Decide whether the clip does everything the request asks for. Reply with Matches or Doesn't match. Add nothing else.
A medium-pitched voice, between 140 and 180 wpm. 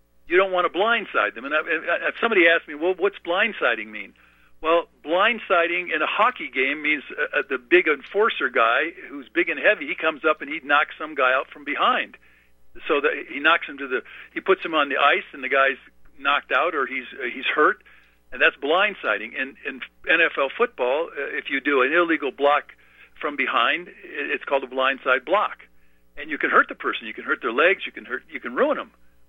Doesn't match